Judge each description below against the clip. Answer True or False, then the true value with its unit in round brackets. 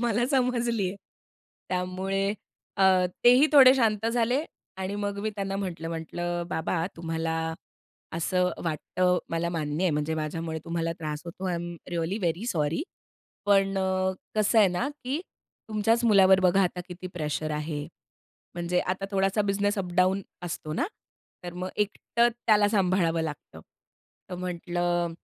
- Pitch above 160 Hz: True (185 Hz)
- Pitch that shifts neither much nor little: True (3.3 semitones)